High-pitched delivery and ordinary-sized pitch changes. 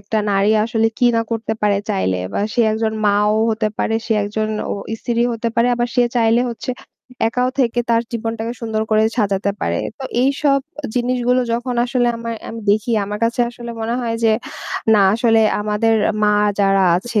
No: high, 225 Hz; narrow, 2.2 semitones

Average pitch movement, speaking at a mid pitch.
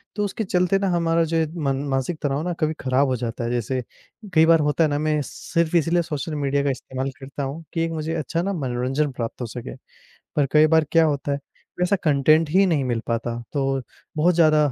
Yes: average, 3.6 semitones; medium, 150 Hz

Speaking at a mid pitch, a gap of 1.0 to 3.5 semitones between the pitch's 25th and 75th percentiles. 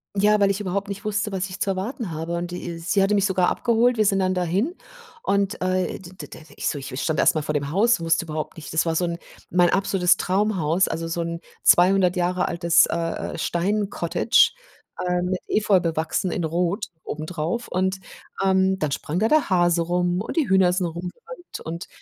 Yes: medium, 180 Hz; average, 2.8 semitones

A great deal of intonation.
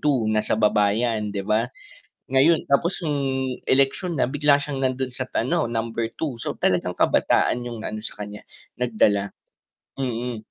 No: average, 4.1 semitones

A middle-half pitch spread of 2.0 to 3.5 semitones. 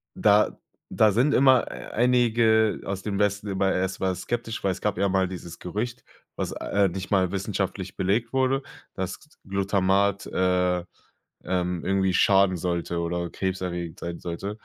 Yes: narrow, 2.5 semitones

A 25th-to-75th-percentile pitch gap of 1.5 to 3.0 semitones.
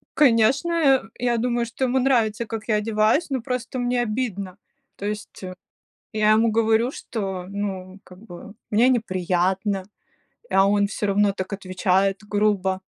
No: average, 3.7 semitones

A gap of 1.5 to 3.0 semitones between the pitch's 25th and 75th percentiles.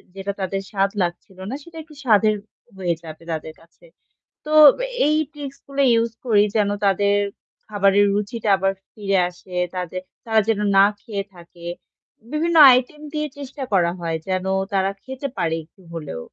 No: average, 5.1 semitones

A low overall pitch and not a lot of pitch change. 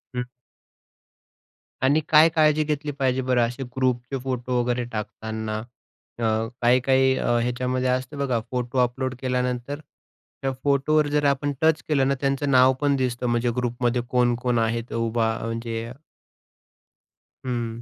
Yes: low, 125 Hz; narrow, 2.3 semitones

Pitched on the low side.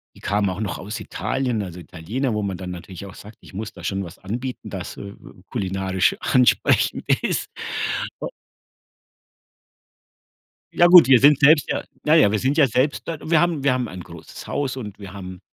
Yes: low, 105 Hz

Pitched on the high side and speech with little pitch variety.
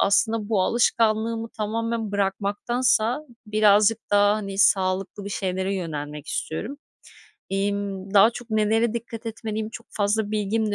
Yes: high, 210 Hz; narrow, 2.3 semitones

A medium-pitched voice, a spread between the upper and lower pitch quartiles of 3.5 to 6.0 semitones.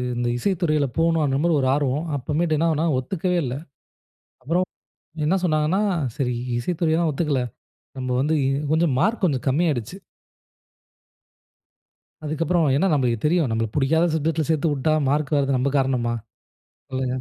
Yes: medium, 150 Hz; average, 3.9 semitones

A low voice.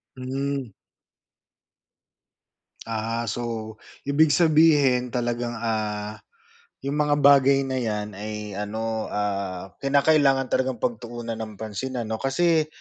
Yes: low, 120 Hz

